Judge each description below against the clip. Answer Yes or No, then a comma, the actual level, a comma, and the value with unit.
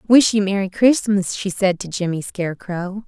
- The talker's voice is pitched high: Yes, high, 195 Hz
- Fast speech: No, average, 175 wpm